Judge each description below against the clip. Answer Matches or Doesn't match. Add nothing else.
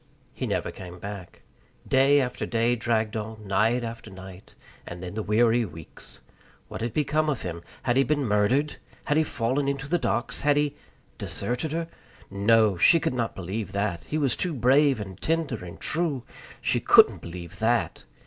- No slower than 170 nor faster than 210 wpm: Matches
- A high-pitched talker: Doesn't match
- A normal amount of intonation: Doesn't match